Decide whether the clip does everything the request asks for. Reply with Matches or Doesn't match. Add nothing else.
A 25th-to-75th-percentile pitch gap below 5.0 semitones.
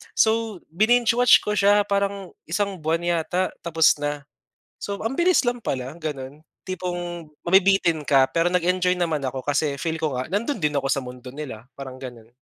Doesn't match